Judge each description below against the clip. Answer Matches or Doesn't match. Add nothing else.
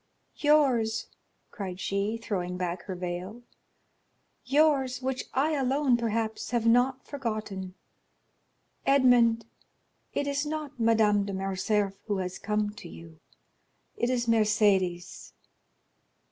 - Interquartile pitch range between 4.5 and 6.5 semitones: Matches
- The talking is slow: Matches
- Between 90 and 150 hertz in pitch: Doesn't match